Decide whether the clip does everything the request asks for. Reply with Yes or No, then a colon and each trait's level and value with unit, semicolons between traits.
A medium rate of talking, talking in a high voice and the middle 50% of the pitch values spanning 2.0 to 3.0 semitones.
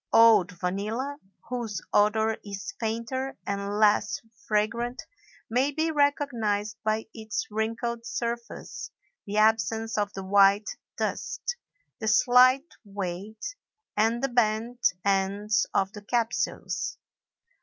No: slow, 110 wpm; high, 220 Hz; narrow, 2.6 semitones